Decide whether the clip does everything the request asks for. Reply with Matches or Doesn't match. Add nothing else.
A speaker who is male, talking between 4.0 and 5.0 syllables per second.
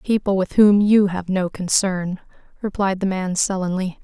Doesn't match